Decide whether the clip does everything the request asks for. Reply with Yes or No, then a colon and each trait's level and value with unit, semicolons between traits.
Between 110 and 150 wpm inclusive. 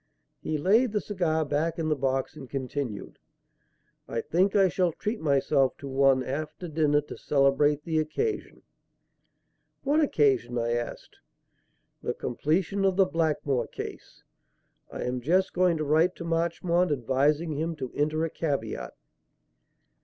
Yes: average, 145 wpm